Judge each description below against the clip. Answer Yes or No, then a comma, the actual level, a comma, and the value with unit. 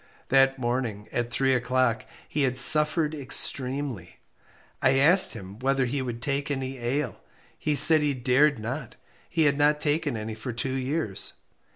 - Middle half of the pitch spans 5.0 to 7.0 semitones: No, average, 3.2 semitones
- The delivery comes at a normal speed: Yes, average, 160 wpm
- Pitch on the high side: No, low, 135 Hz